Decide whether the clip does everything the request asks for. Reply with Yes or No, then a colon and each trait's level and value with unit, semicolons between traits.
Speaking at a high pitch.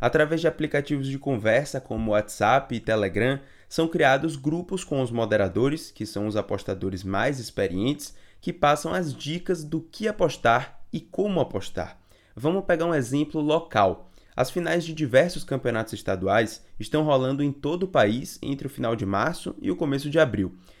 No: low, 135 Hz